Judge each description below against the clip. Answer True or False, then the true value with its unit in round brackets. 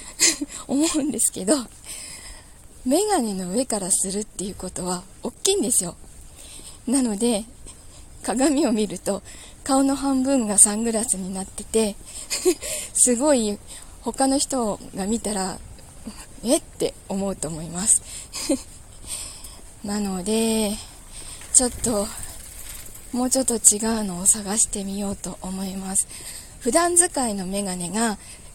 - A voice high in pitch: True (215 Hz)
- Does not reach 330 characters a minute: True (230 characters per minute)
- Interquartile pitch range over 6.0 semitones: False (5.3 semitones)